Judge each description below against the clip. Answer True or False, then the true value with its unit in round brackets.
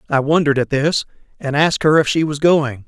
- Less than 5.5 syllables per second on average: False (6.0 syllables/s)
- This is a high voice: False (150 Hz)